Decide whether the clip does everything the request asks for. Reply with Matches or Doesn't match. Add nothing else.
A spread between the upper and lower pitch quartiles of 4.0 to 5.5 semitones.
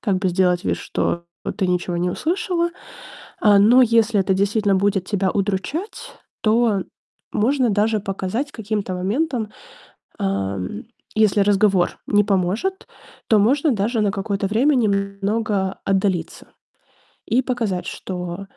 Doesn't match